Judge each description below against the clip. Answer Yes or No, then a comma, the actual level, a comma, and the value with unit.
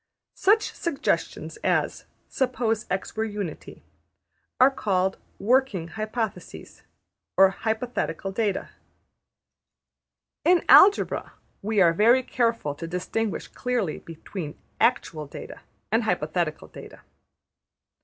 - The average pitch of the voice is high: Yes, high, 215 Hz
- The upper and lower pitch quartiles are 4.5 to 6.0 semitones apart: Yes, average, 4.9 semitones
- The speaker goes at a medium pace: No, slow, 95 wpm